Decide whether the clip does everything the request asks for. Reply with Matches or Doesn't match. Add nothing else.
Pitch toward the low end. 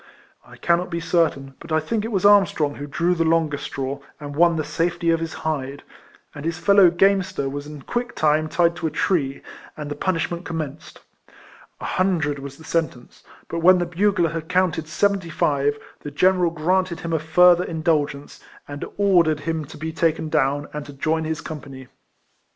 Doesn't match